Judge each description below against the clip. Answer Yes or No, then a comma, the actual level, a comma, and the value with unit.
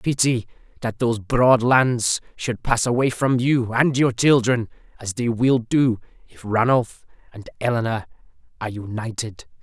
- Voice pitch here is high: No, low, 115 Hz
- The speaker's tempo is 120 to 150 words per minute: Yes, average, 145 wpm